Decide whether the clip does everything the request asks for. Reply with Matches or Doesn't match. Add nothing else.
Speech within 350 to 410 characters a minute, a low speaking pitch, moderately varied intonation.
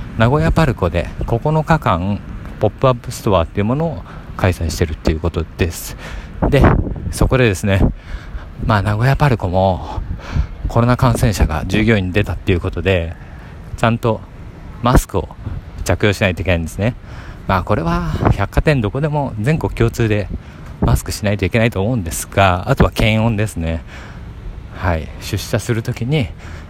Doesn't match